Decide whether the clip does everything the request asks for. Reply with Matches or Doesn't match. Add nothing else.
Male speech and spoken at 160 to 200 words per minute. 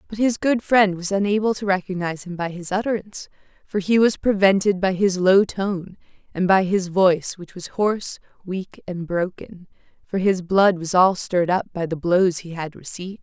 Doesn't match